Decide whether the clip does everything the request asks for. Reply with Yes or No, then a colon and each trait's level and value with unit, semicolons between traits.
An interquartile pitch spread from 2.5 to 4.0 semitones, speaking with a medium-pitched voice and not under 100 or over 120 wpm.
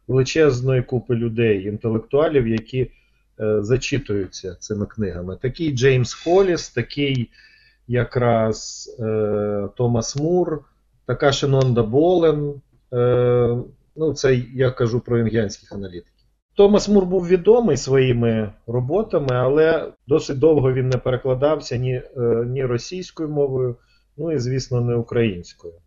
No: average, 3.7 semitones; low, 125 Hz; average, 115 wpm